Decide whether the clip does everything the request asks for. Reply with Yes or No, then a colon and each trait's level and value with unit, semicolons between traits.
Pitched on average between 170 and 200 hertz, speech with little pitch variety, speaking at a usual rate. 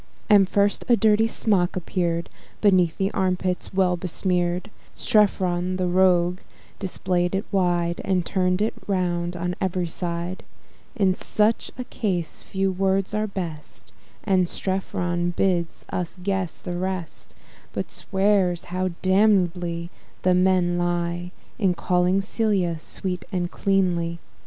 No: medium, 185 Hz; narrow, 1.7 semitones; slow, 130 wpm